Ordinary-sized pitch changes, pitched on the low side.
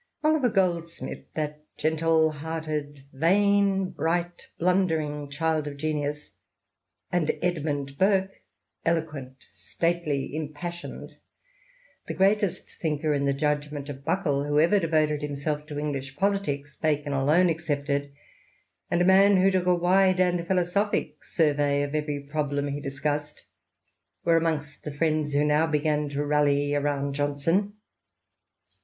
No: average, 3.3 semitones; medium, 155 Hz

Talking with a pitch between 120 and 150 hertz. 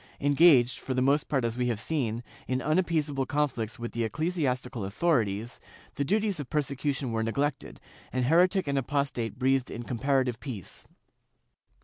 Yes: low, 135 Hz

